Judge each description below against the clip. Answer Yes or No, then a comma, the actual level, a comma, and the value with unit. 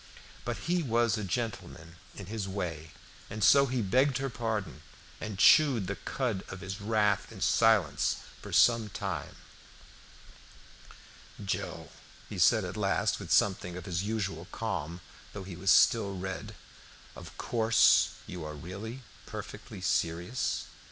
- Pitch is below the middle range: Yes, low, 100 Hz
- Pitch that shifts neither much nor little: Yes, average, 3.9 semitones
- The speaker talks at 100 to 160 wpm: Yes, average, 140 wpm